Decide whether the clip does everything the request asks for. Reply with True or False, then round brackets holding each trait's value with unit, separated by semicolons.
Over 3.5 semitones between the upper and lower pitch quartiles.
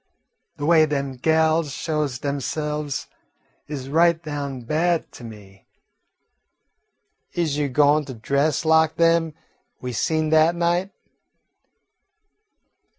False (2.5 semitones)